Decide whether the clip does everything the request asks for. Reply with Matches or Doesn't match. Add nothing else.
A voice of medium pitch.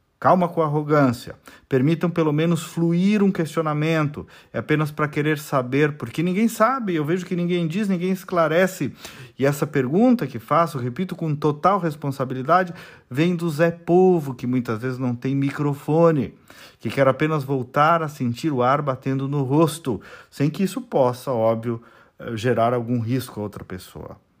Matches